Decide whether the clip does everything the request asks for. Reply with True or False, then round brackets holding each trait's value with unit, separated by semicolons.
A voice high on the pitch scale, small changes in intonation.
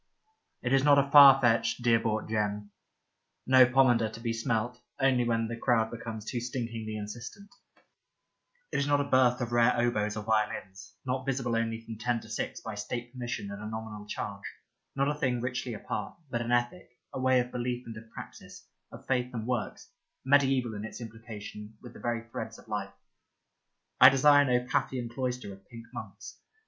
False (120 Hz; 2.3 semitones)